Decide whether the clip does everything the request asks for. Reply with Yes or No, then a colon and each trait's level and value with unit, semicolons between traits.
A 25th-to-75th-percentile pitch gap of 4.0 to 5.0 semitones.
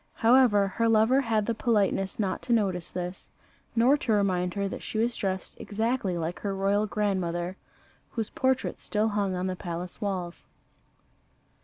No: average, 3.4 semitones